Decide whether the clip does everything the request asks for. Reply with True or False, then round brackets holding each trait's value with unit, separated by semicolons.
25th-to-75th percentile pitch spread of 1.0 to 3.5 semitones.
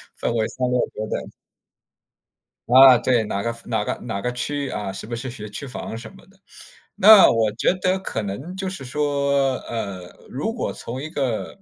False (4.3 semitones)